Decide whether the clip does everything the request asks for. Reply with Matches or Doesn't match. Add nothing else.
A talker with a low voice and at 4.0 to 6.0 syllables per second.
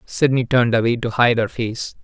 Matches